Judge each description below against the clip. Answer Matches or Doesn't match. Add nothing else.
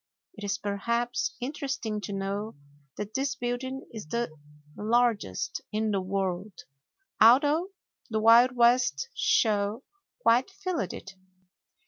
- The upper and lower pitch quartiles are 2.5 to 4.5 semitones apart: Matches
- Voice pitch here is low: Doesn't match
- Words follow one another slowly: Matches